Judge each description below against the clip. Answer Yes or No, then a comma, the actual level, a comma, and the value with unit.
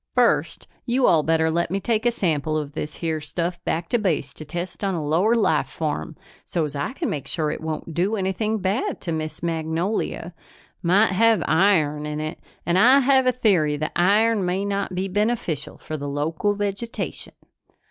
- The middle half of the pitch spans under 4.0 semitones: No, average, 4.9 semitones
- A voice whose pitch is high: No, medium, 175 Hz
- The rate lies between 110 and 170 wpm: No, average, 190 wpm